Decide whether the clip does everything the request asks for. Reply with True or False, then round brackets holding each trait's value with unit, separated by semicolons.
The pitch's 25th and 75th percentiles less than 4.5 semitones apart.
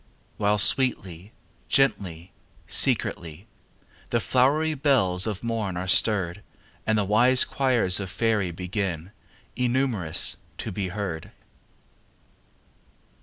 False (4.9 semitones)